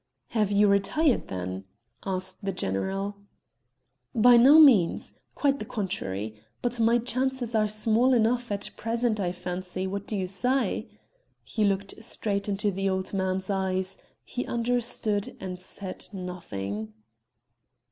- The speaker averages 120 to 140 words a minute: Yes, slow, 135 wpm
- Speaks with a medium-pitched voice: No, high, 200 Hz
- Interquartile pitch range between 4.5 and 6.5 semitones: No, average, 3.8 semitones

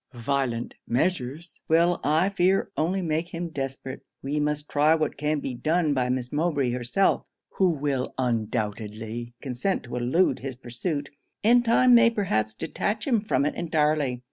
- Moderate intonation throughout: No, wide, 5.7 semitones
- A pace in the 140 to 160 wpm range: Yes, average, 155 wpm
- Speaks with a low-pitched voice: No, medium, 145 Hz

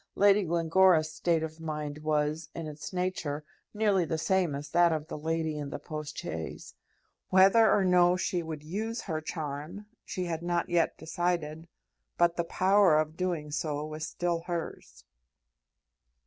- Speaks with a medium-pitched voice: Yes, medium, 165 Hz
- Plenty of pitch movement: No, average, 2.7 semitones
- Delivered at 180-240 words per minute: No, average, 160 wpm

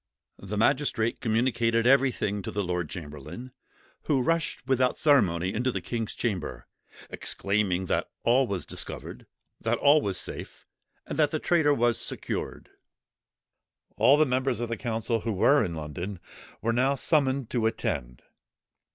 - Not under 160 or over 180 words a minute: No, average, 145 wpm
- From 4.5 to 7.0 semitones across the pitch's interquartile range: Yes, average, 5.2 semitones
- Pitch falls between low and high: No, low, 115 Hz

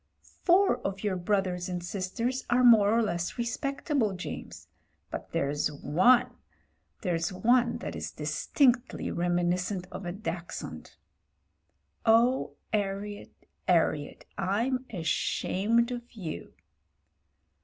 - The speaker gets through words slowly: Yes, slow, 110 wpm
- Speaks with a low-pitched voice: No, high, 200 Hz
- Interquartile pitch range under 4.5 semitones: No, average, 5.1 semitones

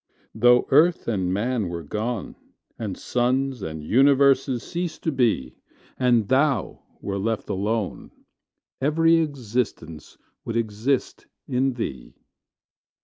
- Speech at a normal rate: No, slow, 110 wpm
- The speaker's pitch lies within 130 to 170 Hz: No, low, 120 Hz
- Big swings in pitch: No, average, 4.7 semitones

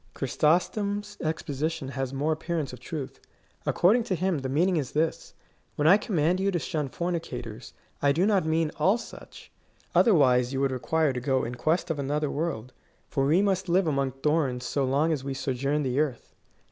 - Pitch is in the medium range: Yes, medium, 150 Hz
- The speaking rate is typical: Yes, average, 190 wpm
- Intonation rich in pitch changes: No, average, 4.3 semitones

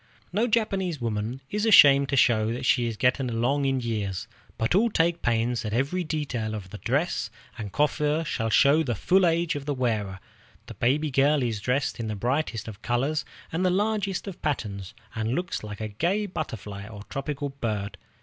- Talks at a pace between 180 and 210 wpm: Yes, average, 190 wpm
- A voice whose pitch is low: Yes, low, 130 Hz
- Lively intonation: Yes, wide, 5.9 semitones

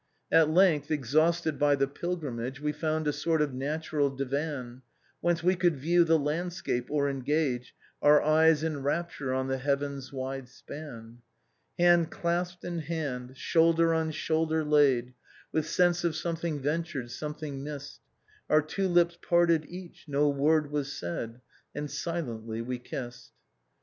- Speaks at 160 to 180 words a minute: No, average, 150 wpm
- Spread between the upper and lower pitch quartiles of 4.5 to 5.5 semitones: No, average, 3.4 semitones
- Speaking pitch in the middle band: Yes, medium, 150 Hz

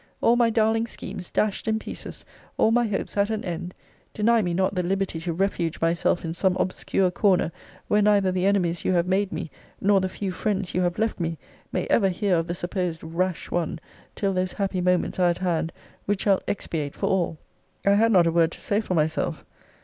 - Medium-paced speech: No, fast, 210 wpm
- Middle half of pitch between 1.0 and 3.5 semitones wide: Yes, average, 2.8 semitones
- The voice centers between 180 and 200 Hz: Yes, medium, 185 Hz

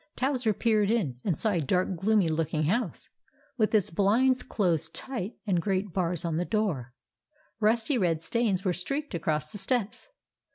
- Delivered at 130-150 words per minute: No, average, 165 wpm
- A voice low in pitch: No, high, 195 Hz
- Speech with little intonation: No, average, 4.9 semitones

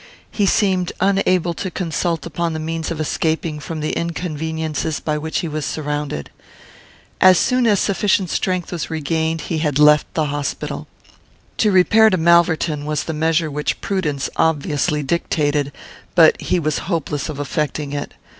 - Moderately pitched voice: Yes, medium, 160 Hz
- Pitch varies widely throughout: No, narrow, 2.5 semitones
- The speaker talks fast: No, average, 155 wpm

